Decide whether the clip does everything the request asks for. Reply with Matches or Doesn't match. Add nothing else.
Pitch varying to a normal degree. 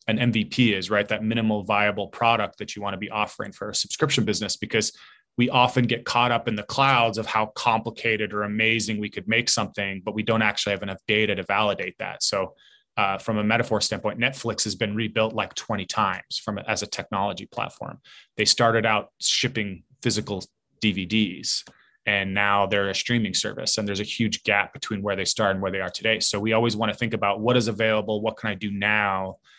Doesn't match